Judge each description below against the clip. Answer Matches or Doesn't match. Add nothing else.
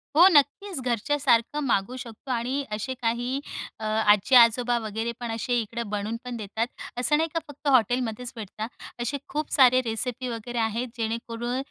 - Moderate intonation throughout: Doesn't match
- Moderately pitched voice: Doesn't match